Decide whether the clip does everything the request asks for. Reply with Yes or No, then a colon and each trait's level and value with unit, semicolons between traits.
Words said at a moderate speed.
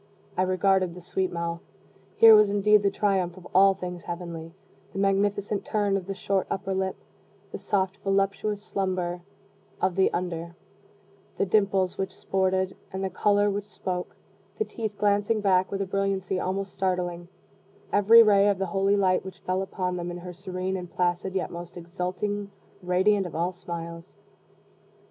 Yes: average, 165 wpm